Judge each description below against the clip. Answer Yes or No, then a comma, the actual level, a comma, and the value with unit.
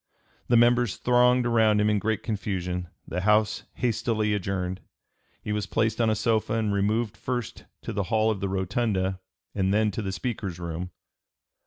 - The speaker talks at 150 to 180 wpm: Yes, average, 170 wpm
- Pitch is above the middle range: No, low, 105 Hz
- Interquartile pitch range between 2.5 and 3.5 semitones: Yes, average, 2.8 semitones